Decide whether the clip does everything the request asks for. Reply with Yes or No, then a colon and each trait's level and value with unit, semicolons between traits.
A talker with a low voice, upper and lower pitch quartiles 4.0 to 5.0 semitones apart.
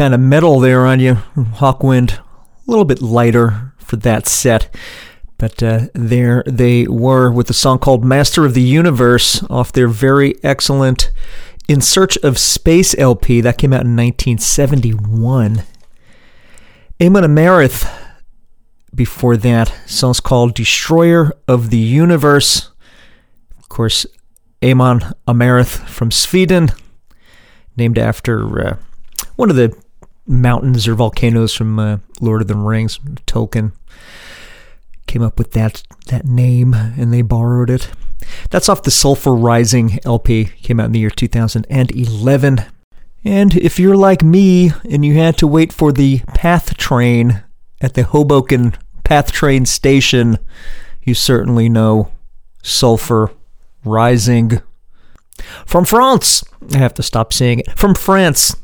No: low, 125 Hz; average, 3.4 semitones